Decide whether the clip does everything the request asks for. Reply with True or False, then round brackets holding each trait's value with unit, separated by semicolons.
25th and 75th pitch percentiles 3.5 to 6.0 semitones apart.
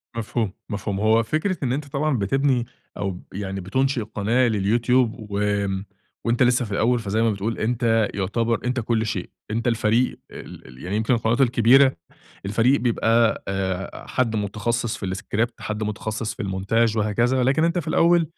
False (3.1 semitones)